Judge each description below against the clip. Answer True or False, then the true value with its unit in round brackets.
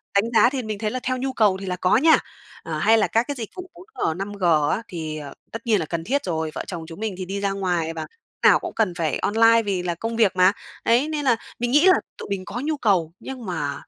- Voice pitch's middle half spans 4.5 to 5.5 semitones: True (5.2 semitones)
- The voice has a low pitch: False (205 Hz)